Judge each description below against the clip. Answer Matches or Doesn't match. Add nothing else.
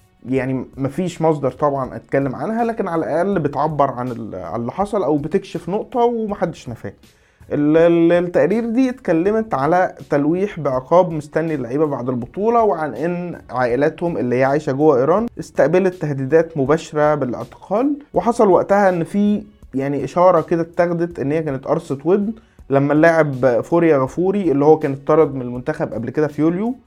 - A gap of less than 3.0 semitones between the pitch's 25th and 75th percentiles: Doesn't match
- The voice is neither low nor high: Matches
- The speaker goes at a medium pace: Doesn't match